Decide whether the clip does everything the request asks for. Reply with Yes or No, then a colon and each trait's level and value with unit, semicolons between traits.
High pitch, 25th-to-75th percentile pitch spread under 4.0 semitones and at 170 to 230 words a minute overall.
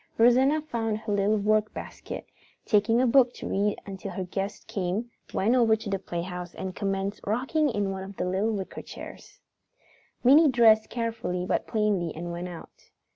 Yes: high, 210 Hz; average, 3.4 semitones; average, 175 wpm